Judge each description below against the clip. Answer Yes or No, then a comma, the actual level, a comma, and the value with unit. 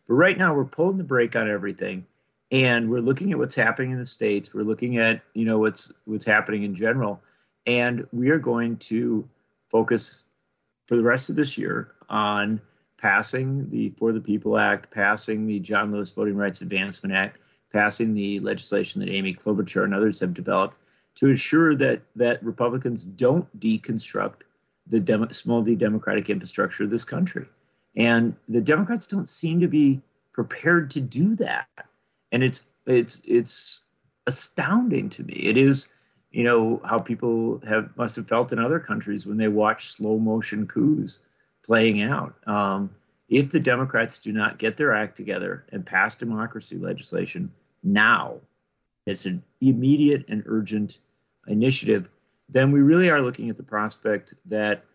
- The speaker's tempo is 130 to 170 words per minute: Yes, average, 165 wpm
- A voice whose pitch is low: Yes, low, 115 Hz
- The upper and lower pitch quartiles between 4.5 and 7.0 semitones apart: No, average, 3.8 semitones